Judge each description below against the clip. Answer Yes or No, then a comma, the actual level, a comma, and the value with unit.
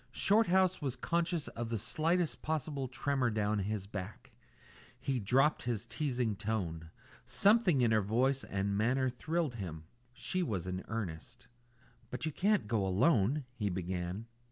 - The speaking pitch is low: Yes, low, 120 Hz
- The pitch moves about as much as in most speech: No, wide, 6.8 semitones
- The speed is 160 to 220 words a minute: No, average, 150 wpm